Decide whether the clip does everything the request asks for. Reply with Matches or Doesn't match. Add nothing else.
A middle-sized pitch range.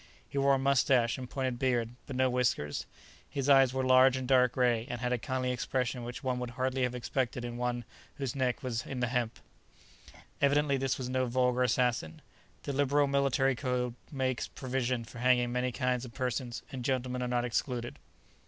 Doesn't match